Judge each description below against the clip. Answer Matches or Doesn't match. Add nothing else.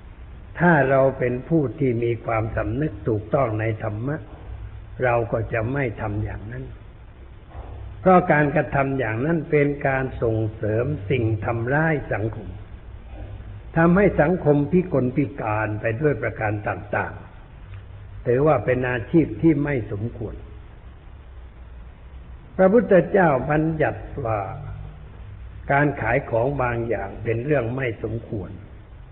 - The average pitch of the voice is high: Doesn't match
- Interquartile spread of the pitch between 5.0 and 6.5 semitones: Matches